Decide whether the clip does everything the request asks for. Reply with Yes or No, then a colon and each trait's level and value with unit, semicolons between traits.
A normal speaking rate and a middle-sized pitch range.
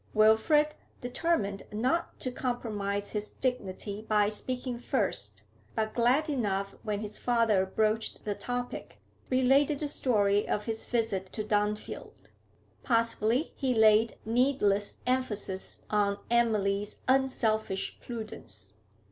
No: slow, 115 wpm; average, 3.3 semitones